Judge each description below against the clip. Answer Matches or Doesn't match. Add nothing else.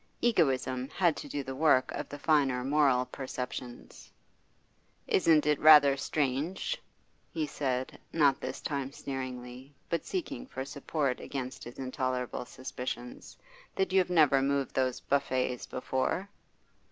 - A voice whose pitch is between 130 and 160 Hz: Matches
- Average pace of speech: Doesn't match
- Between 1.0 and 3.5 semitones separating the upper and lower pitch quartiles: Matches